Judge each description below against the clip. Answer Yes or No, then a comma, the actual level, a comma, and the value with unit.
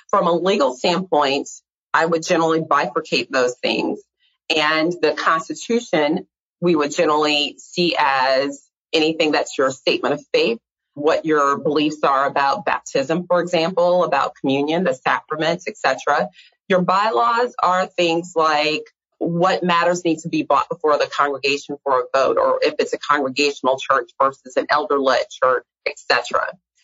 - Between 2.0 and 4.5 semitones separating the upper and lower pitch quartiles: Yes, average, 3.5 semitones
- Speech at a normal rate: Yes, average, 150 wpm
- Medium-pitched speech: Yes, medium, 160 Hz